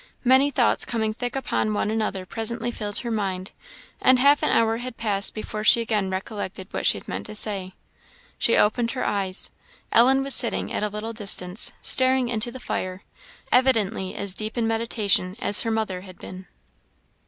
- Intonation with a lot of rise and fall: No, average, 3.2 semitones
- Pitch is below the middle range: No, high, 220 Hz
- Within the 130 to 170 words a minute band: No, average, 180 wpm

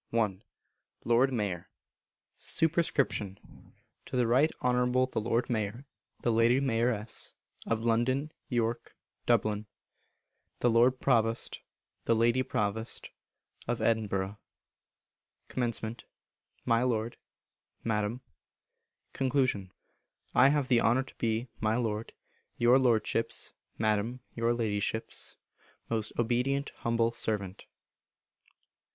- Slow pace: Yes, slow, 100 wpm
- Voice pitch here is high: No, low, 115 Hz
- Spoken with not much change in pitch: Yes, narrow, 2.2 semitones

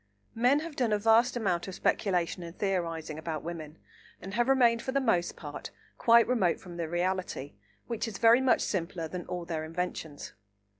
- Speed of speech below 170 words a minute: No, average, 185 wpm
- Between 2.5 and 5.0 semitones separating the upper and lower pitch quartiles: No, wide, 5.6 semitones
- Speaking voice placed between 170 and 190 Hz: Yes, medium, 185 Hz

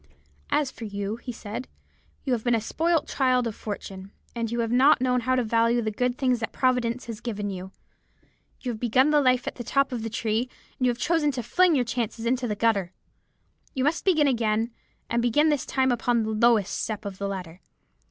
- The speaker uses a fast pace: Yes, fast, 215 wpm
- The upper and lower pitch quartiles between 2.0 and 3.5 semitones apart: Yes, average, 2.9 semitones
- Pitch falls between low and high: No, high, 235 Hz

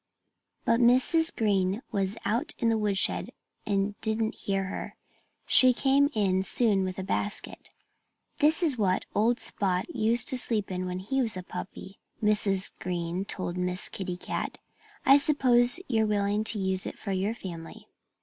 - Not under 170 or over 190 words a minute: No, average, 160 wpm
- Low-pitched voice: No, high, 205 Hz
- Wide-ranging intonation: No, average, 4.0 semitones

